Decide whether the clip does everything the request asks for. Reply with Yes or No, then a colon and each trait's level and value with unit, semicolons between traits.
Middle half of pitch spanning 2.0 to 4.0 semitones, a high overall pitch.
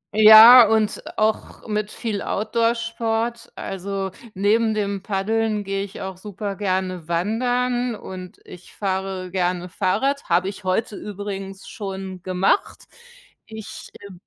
Yes: average, 2.8 semitones; high, 200 Hz